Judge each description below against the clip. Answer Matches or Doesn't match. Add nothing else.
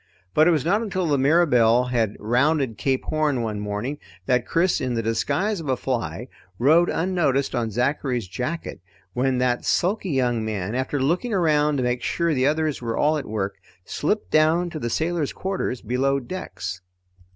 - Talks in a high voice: Doesn't match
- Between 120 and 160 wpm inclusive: Doesn't match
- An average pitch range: Matches